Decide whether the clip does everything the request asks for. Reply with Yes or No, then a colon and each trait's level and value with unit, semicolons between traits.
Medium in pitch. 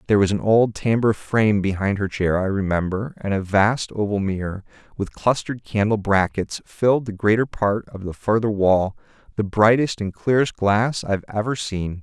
No: low, 105 Hz